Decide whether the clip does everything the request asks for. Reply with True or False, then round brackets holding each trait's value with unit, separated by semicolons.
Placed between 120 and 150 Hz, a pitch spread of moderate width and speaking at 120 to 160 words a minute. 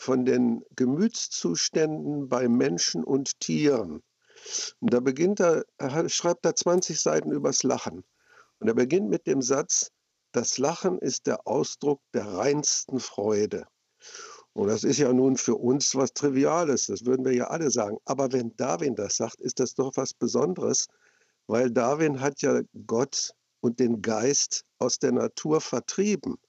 True (135 Hz; 4.7 semitones; 155 wpm)